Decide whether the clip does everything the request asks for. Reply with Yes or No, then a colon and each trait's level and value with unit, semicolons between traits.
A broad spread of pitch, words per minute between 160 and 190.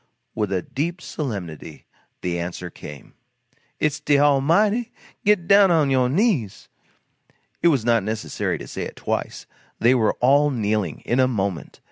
No: wide, 6.9 semitones; average, 145 wpm